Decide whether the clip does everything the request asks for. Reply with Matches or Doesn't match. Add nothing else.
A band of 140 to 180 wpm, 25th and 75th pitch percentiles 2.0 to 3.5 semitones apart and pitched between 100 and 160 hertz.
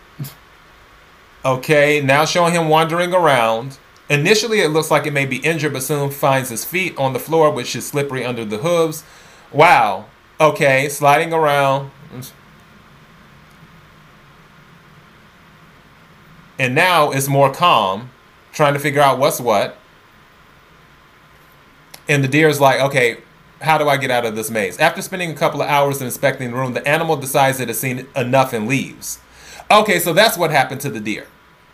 Matches